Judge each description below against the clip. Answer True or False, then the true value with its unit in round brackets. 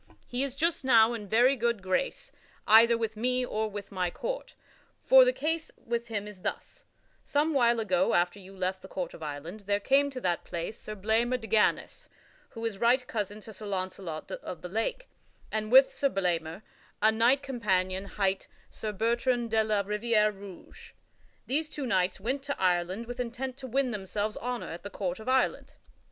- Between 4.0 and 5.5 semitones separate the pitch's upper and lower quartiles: True (4.4 semitones)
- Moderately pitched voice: False (220 Hz)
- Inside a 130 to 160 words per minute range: False (190 wpm)